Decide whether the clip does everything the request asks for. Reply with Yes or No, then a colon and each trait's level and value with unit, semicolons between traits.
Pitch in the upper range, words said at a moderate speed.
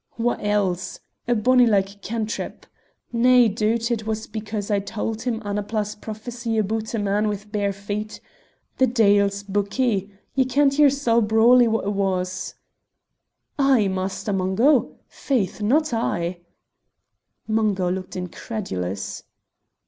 No: high, 215 Hz; slow, 125 wpm